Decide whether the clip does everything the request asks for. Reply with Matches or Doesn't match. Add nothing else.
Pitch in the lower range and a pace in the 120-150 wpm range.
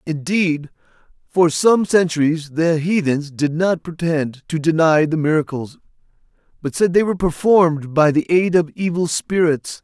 Doesn't match